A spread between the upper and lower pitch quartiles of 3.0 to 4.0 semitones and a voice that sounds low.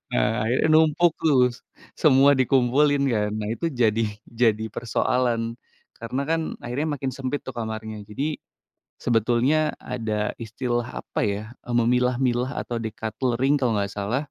Yes: average, 3.4 semitones; low, 120 Hz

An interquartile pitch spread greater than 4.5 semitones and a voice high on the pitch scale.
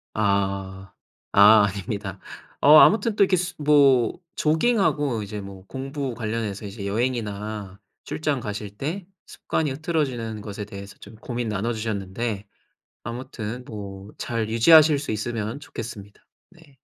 No: average, 5.3 semitones; low, 115 Hz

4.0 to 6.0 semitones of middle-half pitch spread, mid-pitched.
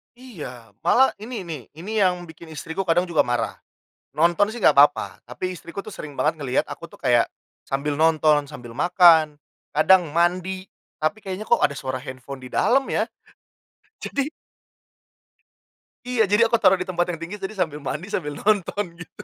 Yes: average, 4.6 semitones; medium, 170 Hz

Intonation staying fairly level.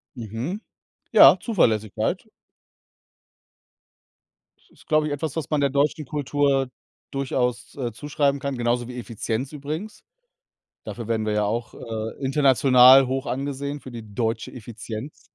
No: average, 3.7 semitones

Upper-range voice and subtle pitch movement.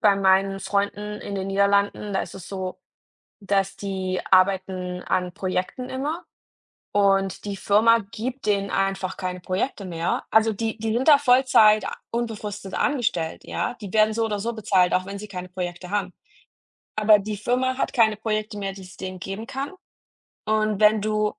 Yes: high, 200 Hz; narrow, 2.3 semitones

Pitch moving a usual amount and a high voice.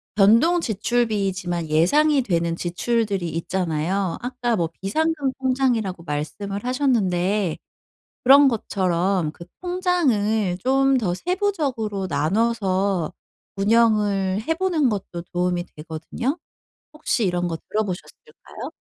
No: wide, 6.3 semitones; high, 205 Hz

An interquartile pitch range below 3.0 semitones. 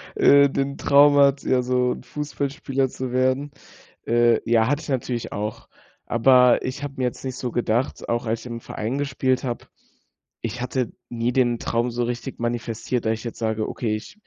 Yes: narrow, 2.4 semitones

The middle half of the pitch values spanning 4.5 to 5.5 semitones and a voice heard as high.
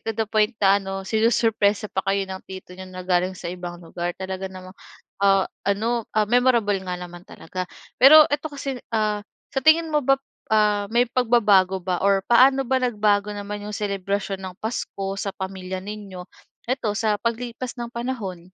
No: average, 3.8 semitones; high, 205 Hz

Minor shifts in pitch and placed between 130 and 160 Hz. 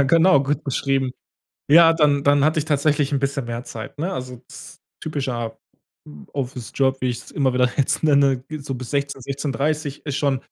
Yes: narrow, 2.3 semitones; medium, 140 Hz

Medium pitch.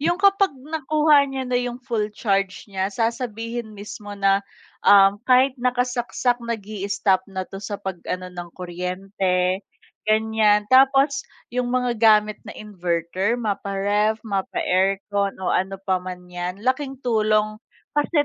No: high, 210 Hz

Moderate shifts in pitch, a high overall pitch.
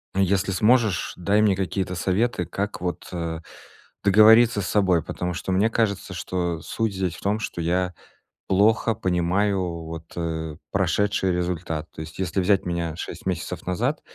No: average, 3.0 semitones; very low, 95 Hz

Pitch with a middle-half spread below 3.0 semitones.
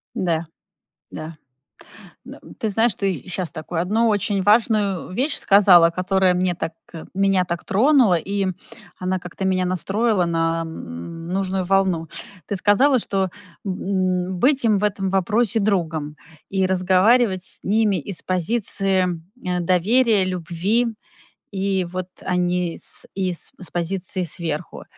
Yes: narrow, 2.5 semitones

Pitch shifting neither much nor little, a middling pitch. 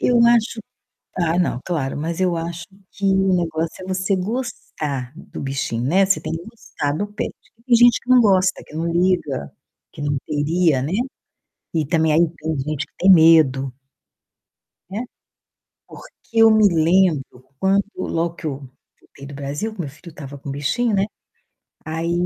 Yes: average, 4.7 semitones; medium, 170 Hz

